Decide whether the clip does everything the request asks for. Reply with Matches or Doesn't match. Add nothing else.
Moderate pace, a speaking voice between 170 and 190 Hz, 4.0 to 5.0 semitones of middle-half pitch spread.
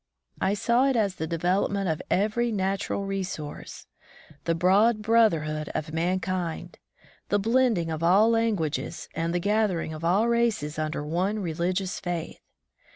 Matches